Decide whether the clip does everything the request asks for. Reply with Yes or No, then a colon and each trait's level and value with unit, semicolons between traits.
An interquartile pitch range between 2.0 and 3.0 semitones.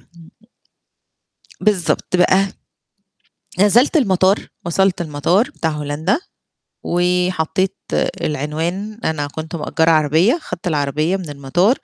No: average, 3.8 semitones